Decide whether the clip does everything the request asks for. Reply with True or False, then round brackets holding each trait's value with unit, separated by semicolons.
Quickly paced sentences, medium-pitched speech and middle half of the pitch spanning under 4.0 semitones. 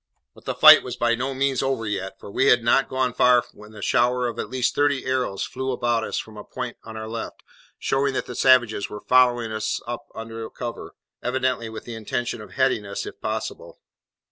False (215 wpm; 120 Hz; 2.6 semitones)